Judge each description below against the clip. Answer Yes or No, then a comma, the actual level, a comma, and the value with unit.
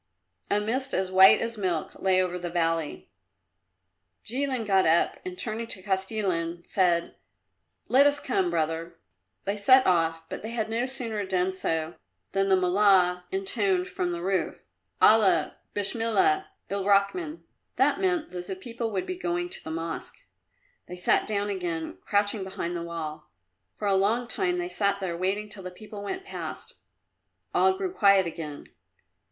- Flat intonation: No, average, 4.1 semitones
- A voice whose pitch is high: Yes, high, 195 Hz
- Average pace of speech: Yes, average, 160 wpm